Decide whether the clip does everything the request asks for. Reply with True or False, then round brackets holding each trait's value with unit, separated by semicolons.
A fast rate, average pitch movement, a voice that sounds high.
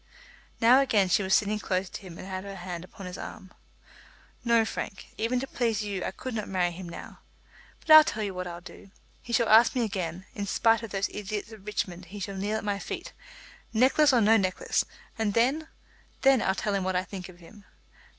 True (220 wpm; 3.3 semitones; 205 Hz)